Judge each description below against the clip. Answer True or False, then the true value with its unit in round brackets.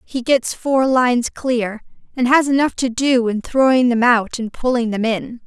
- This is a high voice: True (245 Hz)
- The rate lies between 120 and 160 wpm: False (200 wpm)